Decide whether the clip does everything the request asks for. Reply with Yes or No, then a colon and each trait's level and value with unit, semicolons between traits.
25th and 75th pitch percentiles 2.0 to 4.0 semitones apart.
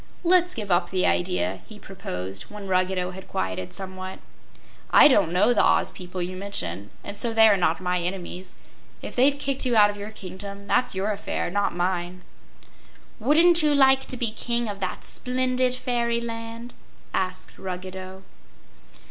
No: average, 4.5 semitones